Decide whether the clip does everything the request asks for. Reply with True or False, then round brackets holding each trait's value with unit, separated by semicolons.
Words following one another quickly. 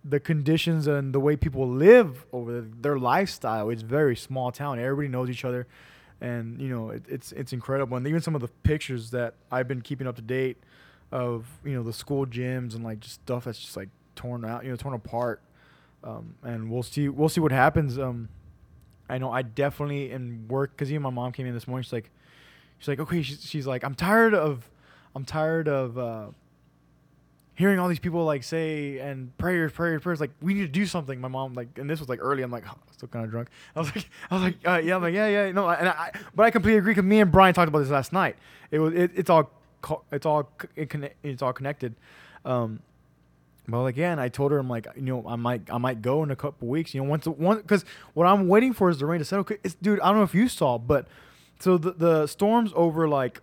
True (245 wpm)